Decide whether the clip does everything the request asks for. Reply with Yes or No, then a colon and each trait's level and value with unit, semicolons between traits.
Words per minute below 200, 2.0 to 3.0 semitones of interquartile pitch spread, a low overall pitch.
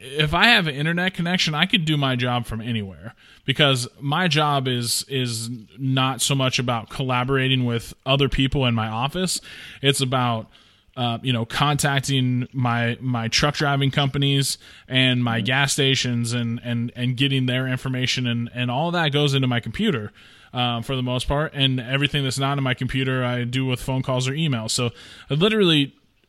Yes: average, 185 wpm; narrow, 2.5 semitones; low, 130 Hz